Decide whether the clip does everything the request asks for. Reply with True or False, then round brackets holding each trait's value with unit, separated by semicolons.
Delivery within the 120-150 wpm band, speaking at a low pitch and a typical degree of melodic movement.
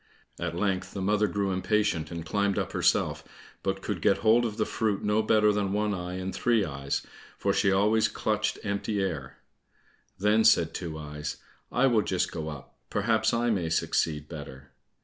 False (180 wpm; 100 Hz; 4.1 semitones)